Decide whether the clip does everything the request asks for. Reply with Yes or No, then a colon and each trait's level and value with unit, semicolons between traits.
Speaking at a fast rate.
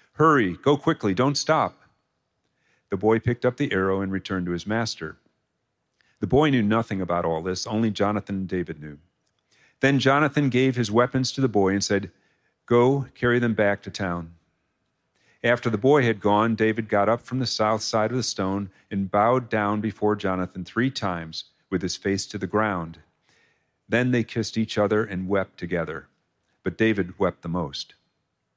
No: average, 180 wpm